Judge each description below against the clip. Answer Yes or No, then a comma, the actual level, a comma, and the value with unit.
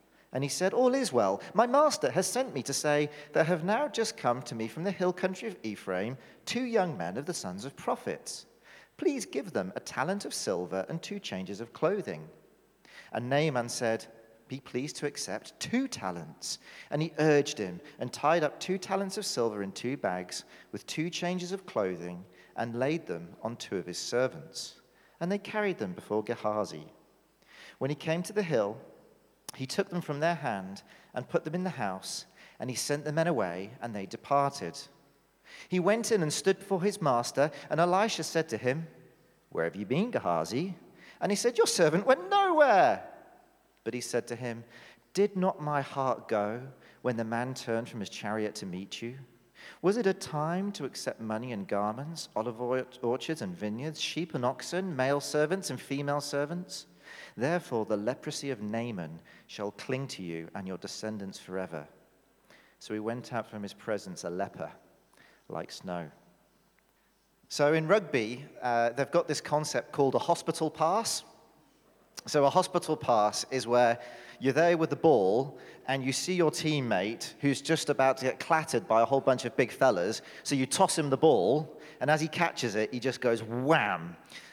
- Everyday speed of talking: Yes, average, 185 wpm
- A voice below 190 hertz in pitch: Yes, medium, 140 Hz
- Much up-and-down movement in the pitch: Yes, wide, 6.6 semitones